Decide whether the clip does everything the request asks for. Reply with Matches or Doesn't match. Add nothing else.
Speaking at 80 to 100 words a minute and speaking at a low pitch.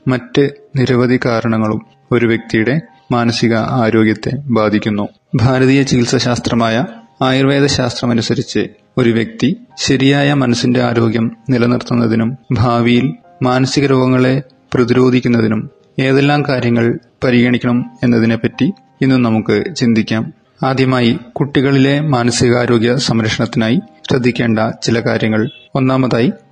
Matches